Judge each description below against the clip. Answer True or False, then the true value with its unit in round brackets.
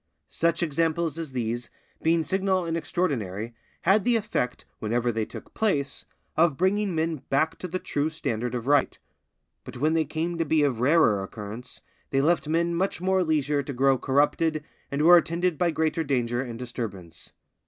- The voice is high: False (155 Hz)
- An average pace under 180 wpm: True (170 wpm)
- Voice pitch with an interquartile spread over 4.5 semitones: True (5.1 semitones)